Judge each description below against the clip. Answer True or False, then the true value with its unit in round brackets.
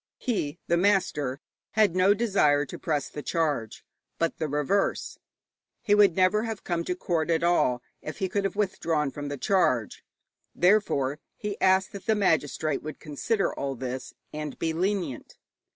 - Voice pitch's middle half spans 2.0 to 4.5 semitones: False (5.2 semitones)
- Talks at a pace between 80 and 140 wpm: False (165 wpm)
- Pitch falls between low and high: True (170 Hz)